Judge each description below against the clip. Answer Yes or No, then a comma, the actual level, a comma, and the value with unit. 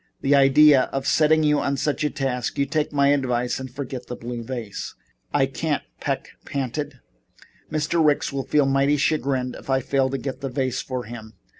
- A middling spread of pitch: No, narrow, 2.3 semitones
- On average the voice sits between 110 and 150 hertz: Yes, low, 135 Hz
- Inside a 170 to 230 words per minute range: Yes, average, 185 wpm